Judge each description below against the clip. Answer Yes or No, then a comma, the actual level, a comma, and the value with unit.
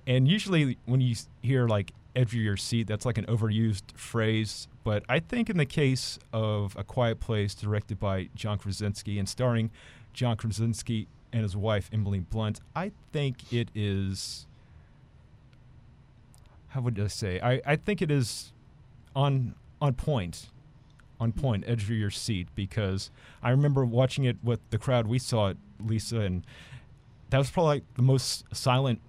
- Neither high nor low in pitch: No, low, 120 Hz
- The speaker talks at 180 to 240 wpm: No, average, 165 wpm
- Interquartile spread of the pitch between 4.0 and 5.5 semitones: No, average, 3.3 semitones